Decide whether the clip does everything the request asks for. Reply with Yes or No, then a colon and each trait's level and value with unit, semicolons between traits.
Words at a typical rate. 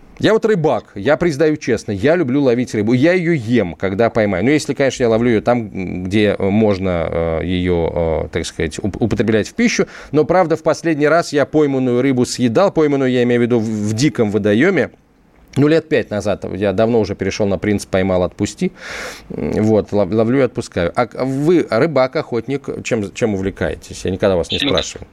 No: fast, 180 wpm